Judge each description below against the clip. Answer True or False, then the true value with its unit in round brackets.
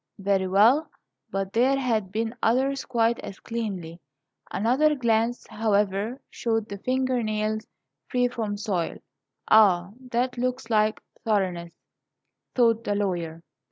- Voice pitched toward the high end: True (220 Hz)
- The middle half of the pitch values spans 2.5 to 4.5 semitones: True (3.5 semitones)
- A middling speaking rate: False (125 wpm)